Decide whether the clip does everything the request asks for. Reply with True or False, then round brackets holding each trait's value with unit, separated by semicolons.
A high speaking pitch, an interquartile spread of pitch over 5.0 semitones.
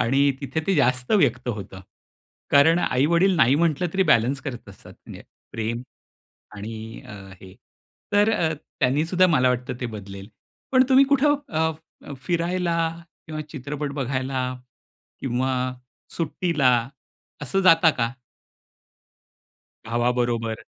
False (140 Hz; 5.6 semitones)